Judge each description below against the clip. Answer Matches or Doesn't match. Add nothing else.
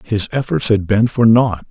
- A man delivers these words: Matches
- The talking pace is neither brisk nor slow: Doesn't match